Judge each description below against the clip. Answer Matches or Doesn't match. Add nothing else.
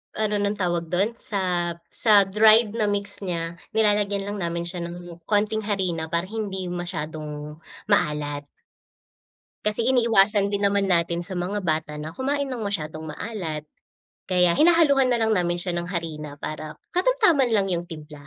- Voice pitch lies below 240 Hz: Matches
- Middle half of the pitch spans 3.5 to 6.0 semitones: Matches